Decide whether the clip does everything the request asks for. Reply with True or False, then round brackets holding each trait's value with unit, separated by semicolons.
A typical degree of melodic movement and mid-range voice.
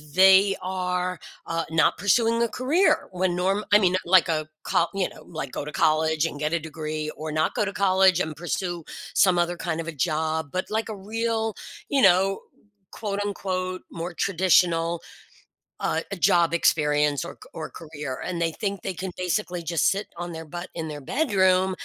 True (3.1 semitones; 180 Hz)